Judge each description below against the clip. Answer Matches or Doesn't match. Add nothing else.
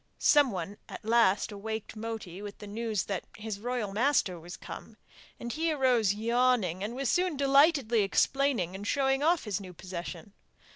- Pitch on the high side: Matches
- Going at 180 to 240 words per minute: Doesn't match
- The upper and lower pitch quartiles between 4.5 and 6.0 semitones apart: Matches